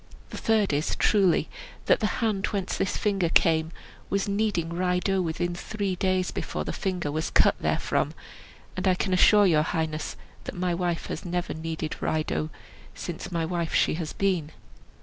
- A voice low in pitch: No, medium, 180 Hz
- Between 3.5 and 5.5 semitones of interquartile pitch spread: No, average, 3.1 semitones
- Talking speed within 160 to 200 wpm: Yes, average, 175 wpm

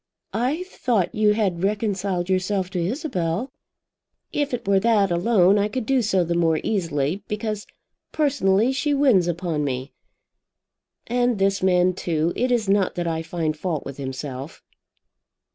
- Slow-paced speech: No, average, 150 wpm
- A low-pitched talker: No, high, 190 Hz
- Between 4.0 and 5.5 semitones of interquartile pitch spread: Yes, average, 4.5 semitones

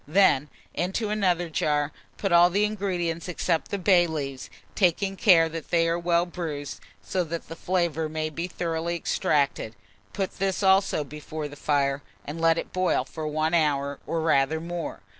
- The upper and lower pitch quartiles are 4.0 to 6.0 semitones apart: No, average, 2.8 semitones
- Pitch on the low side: No, medium, 165 Hz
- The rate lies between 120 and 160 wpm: No, average, 170 wpm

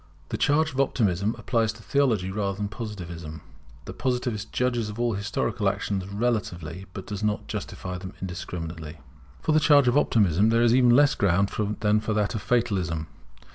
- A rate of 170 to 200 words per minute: Yes, average, 175 wpm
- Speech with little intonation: No, average, 4.3 semitones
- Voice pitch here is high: No, low, 105 Hz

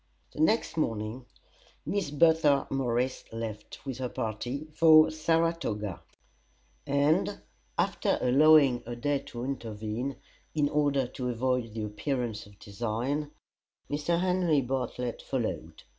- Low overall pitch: Yes, low, 130 Hz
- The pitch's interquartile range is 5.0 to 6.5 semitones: No, average, 4.6 semitones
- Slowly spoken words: Yes, slow, 115 wpm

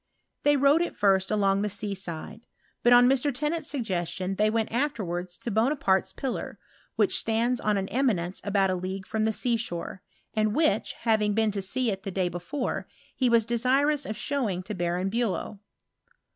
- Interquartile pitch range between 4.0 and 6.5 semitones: Yes, average, 4.4 semitones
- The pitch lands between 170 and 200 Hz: No, high, 215 Hz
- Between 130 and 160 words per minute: No, average, 185 wpm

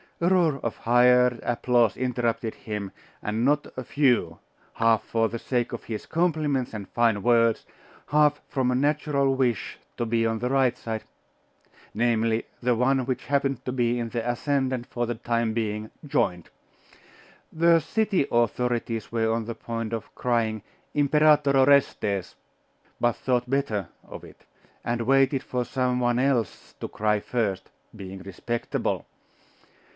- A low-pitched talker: Yes, low, 120 Hz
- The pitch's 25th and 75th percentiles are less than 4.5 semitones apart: Yes, average, 3.0 semitones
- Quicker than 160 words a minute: No, average, 150 wpm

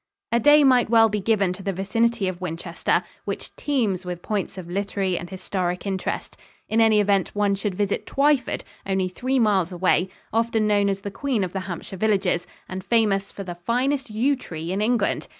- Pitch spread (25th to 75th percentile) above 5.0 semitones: No, average, 3.4 semitones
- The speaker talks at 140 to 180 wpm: No, average, 190 wpm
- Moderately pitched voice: No, high, 200 Hz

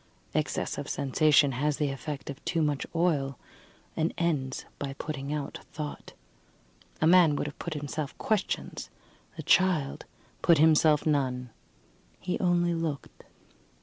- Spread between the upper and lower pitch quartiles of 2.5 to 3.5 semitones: Yes, average, 2.9 semitones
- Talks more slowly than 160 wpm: Yes, slow, 135 wpm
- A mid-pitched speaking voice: Yes, medium, 150 Hz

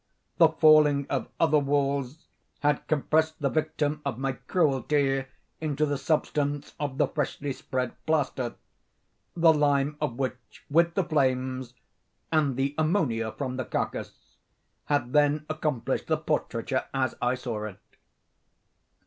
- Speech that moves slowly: Yes, slow, 130 wpm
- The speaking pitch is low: No, medium, 145 Hz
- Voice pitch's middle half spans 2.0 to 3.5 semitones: Yes, average, 2.8 semitones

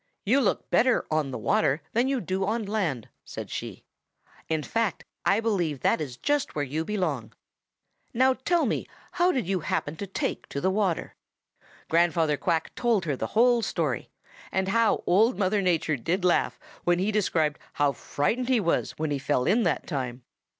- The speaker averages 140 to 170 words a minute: No, average, 180 wpm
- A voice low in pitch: No, medium, 185 Hz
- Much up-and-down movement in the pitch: Yes, wide, 6.6 semitones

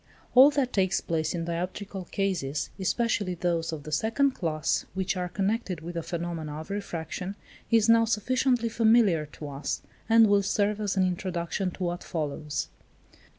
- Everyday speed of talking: Yes, average, 160 wpm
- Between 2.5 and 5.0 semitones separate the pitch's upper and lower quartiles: Yes, average, 4.3 semitones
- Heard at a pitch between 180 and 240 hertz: Yes, medium, 185 Hz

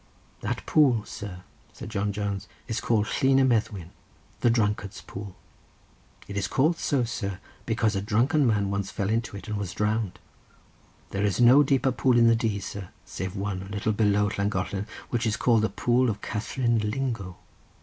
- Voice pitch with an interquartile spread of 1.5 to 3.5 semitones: Yes, average, 3.0 semitones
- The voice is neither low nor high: No, low, 105 Hz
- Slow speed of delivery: No, average, 180 wpm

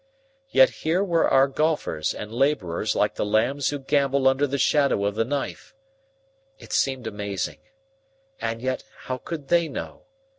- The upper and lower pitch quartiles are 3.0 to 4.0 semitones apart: No, average, 4.4 semitones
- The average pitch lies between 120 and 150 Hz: Yes, low, 135 Hz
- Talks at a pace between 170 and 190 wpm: No, average, 155 wpm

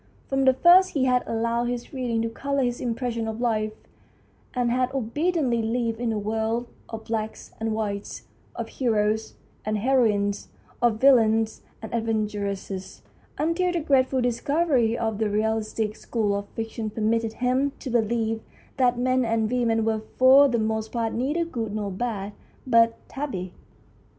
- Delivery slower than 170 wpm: Yes, average, 155 wpm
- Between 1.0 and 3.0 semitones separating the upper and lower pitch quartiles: Yes, narrow, 2.5 semitones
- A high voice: Yes, high, 230 Hz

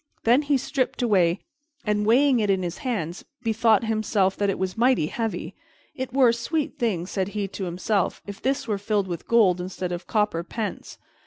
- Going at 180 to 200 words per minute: Yes, average, 190 wpm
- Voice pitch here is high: Yes, high, 210 Hz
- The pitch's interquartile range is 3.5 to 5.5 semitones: Yes, average, 4.0 semitones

